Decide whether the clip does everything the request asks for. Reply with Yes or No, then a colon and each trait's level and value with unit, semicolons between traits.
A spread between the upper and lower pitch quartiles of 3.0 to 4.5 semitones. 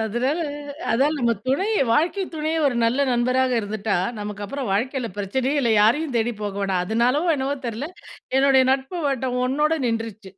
Yes: average, 4.0 semitones